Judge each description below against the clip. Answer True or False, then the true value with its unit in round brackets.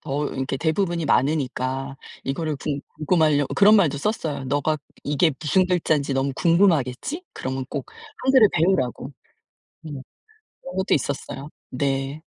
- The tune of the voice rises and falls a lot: False (3.9 semitones)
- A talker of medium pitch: True (150 Hz)